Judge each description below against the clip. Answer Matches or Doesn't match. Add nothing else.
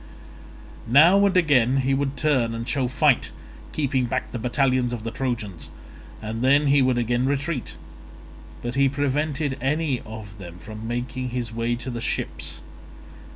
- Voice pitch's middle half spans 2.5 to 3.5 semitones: Matches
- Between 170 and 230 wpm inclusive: Doesn't match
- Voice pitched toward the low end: Matches